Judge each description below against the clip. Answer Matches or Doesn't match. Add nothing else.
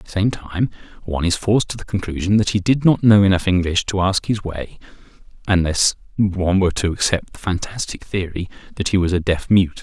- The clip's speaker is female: Doesn't match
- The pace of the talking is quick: Matches